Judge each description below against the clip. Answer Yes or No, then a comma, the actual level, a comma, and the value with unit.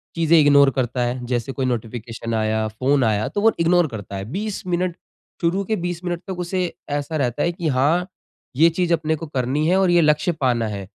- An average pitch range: No, wide, 6.2 semitones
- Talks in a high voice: No, medium, 150 Hz